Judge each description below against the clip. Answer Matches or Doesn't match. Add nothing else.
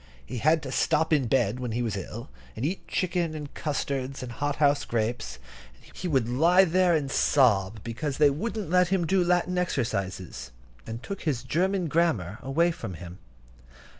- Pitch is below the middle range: Doesn't match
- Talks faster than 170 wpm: Matches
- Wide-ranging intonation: Matches